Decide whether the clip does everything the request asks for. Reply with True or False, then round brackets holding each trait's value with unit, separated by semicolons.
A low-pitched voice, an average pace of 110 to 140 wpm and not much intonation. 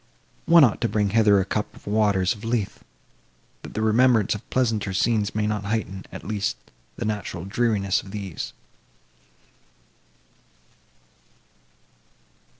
True (105 Hz; 135 wpm; 2.1 semitones)